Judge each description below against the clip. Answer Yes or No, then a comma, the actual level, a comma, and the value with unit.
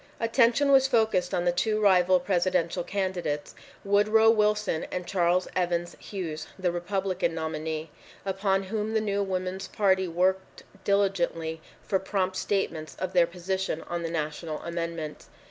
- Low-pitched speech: No, medium, 185 Hz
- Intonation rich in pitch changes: No, average, 2.8 semitones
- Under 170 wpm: Yes, average, 140 wpm